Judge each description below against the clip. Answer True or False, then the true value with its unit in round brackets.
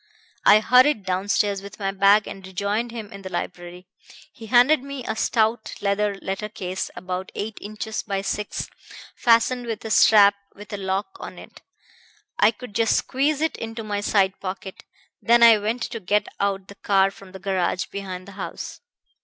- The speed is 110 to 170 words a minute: False (180 wpm)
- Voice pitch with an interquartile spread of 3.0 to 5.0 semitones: False (2.6 semitones)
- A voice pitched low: False (205 Hz)